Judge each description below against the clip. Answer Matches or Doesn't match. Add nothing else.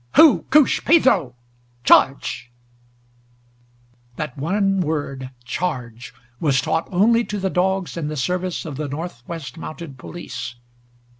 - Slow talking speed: Matches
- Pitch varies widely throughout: Matches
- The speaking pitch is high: Doesn't match